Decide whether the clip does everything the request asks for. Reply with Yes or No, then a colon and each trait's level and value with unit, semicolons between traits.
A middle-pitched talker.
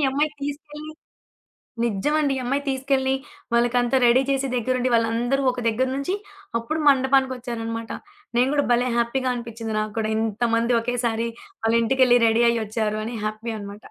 No: high, 240 Hz